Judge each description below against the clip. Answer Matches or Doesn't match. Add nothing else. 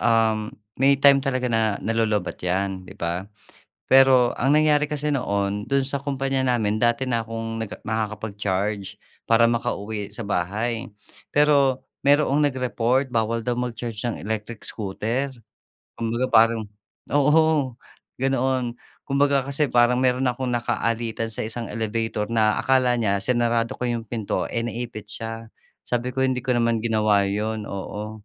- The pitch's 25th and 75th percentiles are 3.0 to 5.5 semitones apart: Matches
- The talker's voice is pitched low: Matches